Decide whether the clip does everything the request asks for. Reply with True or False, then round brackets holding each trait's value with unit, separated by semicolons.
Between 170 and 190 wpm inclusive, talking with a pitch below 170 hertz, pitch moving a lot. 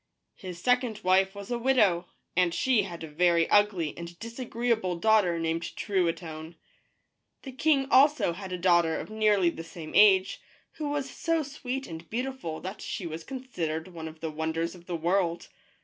False (175 wpm; 185 Hz; 5.8 semitones)